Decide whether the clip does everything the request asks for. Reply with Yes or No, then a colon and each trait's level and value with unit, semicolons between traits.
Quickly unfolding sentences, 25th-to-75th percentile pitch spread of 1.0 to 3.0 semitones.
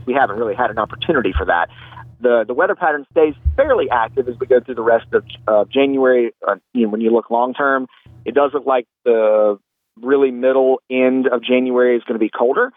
Yes: fast, 220 wpm; average, 2.7 semitones